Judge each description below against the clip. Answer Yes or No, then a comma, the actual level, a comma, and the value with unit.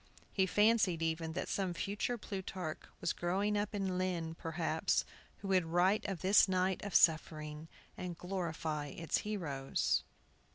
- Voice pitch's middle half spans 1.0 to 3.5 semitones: Yes, average, 3.2 semitones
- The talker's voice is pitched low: No, medium, 180 Hz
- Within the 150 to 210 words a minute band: No, average, 140 wpm